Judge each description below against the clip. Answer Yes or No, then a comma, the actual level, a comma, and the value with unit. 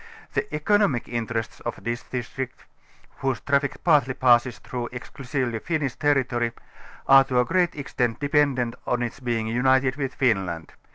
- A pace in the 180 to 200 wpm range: No, average, 145 wpm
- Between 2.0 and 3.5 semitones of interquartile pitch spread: Yes, average, 2.8 semitones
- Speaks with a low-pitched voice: Yes, low, 130 Hz